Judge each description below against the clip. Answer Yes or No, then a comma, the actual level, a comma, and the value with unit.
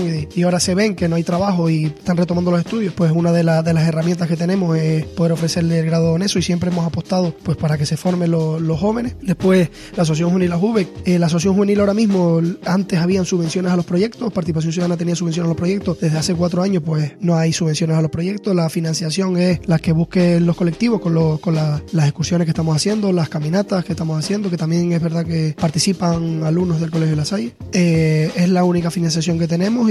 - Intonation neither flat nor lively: No, narrow, 1.9 semitones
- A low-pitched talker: No, medium, 170 Hz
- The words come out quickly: Yes, fast, 235 wpm